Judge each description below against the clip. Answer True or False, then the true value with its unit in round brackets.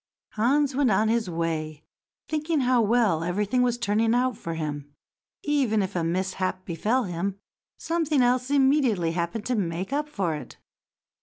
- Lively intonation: True (6.7 semitones)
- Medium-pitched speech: False (215 Hz)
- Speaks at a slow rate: False (155 wpm)